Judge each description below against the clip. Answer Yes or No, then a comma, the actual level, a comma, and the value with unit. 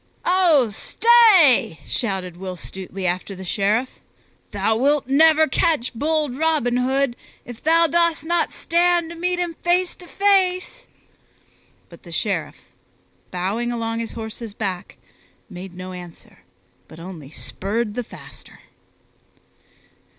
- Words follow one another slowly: Yes, slow, 125 wpm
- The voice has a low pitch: No, very high, 250 Hz